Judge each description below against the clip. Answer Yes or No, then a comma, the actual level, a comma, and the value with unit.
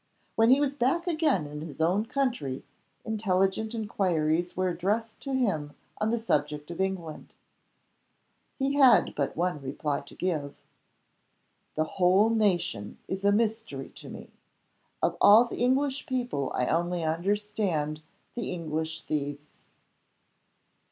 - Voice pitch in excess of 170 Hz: Yes, medium, 185 Hz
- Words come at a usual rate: No, slow, 130 wpm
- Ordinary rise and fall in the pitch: No, wide, 6.5 semitones